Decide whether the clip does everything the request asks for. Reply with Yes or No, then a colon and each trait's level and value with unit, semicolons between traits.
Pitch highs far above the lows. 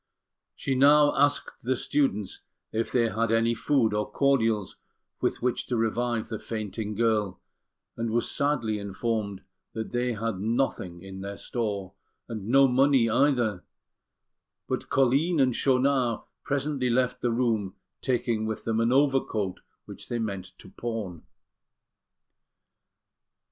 No: average, 3.4 semitones